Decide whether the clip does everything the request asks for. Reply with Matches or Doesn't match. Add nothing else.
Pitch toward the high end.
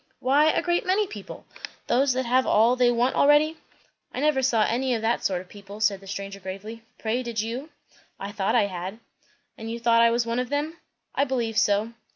Matches